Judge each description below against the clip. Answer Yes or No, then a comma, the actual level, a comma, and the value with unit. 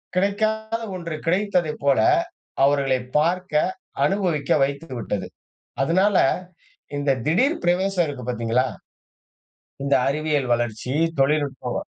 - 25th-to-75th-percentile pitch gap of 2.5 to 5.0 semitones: No, wide, 5.4 semitones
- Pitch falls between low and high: Yes, medium, 155 Hz